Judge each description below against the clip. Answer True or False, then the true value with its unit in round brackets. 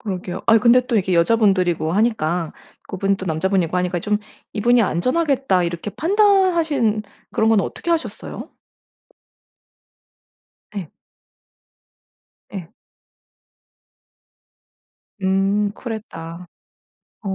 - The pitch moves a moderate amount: True (4.8 semitones)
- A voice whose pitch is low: False (200 Hz)